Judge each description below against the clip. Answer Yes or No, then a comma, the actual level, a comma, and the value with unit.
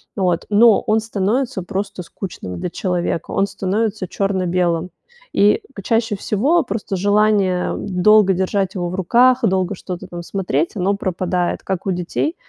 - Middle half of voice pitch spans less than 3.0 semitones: Yes, narrow, 2.6 semitones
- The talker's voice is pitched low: No, high, 195 Hz